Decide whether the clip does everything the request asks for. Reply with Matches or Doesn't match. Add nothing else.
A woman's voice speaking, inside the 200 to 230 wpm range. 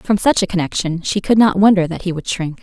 Doesn't match